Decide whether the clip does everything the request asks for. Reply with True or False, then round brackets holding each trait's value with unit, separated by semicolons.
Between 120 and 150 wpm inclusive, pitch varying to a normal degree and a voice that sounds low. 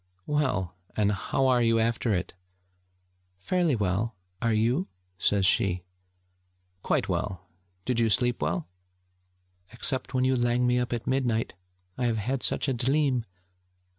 True (140 wpm; 3.8 semitones; 120 Hz)